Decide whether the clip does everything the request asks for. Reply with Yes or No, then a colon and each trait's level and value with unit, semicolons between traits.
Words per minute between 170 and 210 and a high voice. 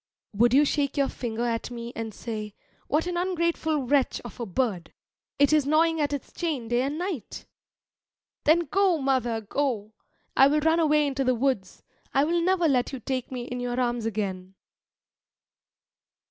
Yes: average, 175 wpm; very high, 265 Hz